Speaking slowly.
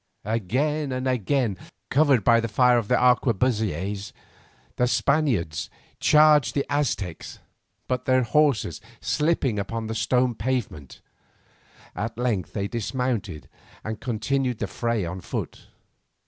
Yes: slow, 120 wpm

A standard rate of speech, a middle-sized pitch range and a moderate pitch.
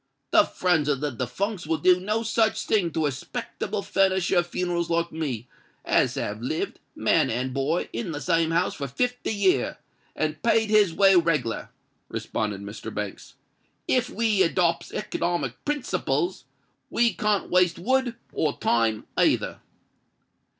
No: average, 150 wpm; wide, 6.3 semitones; medium, 175 Hz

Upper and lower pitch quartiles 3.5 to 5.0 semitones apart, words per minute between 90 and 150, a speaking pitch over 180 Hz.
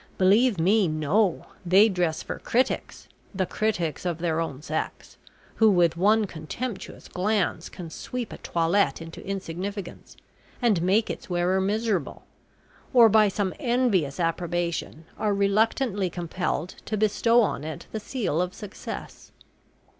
Yes: average, 4.2 semitones; slow, 135 wpm; high, 190 Hz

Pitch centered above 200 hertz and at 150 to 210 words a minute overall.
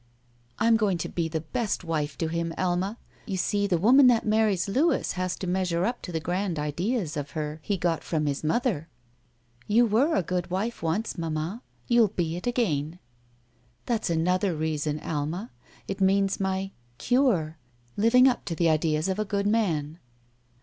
No: medium, 185 Hz; average, 175 wpm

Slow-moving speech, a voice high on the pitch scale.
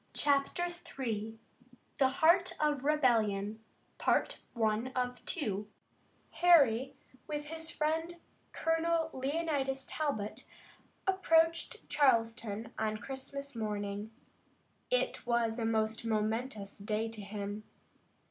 Yes: slow, 85 wpm; very high, 250 Hz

